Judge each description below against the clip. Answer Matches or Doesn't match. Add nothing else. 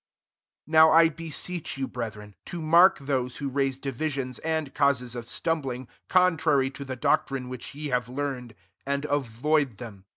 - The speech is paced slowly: Doesn't match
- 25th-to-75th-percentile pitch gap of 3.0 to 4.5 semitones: Matches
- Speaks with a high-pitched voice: Doesn't match